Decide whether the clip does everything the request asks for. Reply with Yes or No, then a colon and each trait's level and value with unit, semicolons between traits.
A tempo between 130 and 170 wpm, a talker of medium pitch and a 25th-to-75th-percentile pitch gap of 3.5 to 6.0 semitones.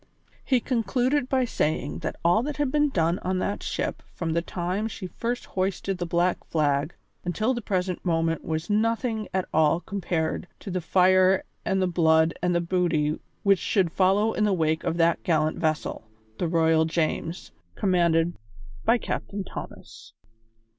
Yes: average, 165 wpm; medium, 180 Hz; average, 3.8 semitones